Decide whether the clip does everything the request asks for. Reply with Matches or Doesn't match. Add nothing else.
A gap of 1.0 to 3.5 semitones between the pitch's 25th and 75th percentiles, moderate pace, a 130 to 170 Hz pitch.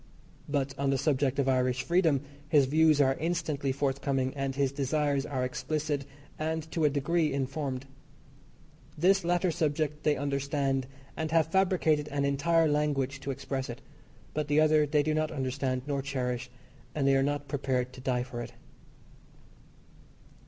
Matches